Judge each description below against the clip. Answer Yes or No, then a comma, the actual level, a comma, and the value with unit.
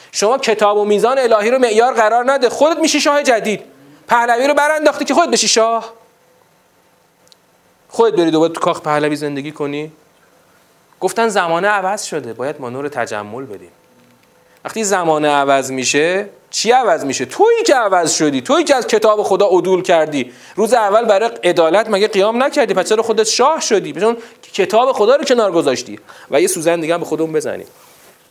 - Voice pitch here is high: Yes, high, 210 Hz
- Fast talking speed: Yes, fast, 170 wpm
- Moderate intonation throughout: No, wide, 6.6 semitones